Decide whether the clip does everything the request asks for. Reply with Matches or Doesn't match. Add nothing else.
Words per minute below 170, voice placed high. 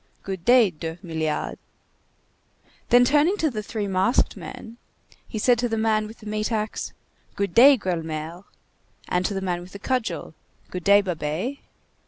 Matches